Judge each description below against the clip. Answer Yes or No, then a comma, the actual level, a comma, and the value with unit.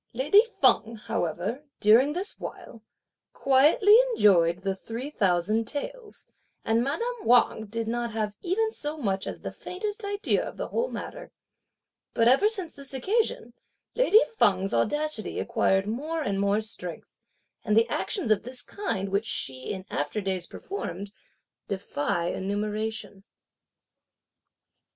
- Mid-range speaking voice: No, high, 230 Hz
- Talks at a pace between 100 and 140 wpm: Yes, slow, 135 wpm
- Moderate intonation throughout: No, wide, 8.2 semitones